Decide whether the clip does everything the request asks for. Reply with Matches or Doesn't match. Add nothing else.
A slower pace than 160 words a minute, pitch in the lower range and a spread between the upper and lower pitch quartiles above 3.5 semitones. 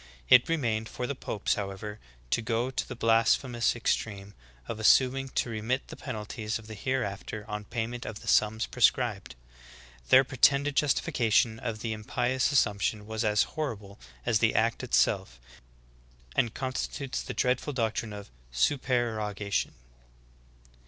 Doesn't match